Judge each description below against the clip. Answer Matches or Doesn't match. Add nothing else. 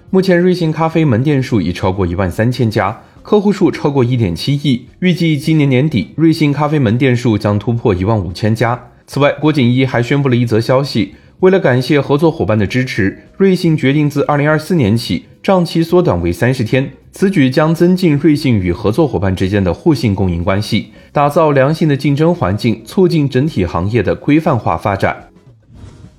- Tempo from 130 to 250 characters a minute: Doesn't match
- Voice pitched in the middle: Doesn't match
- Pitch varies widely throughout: Matches